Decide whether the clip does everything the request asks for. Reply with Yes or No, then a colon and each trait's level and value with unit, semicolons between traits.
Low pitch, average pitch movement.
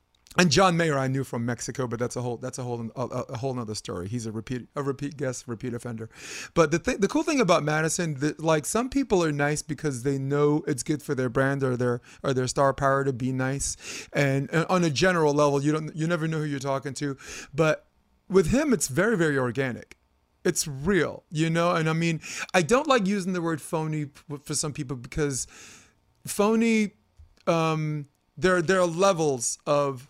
No: medium, 145 Hz; average, 4.3 semitones